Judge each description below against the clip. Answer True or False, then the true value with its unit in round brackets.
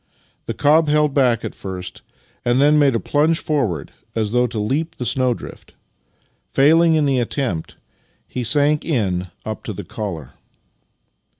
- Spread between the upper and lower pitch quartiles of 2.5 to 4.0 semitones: False (5.3 semitones)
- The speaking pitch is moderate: False (130 Hz)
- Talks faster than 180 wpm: False (155 wpm)